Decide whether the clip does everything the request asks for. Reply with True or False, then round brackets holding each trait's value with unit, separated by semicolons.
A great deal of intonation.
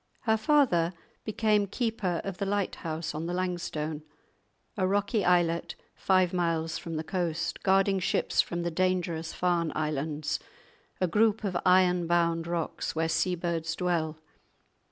False (2.5 semitones)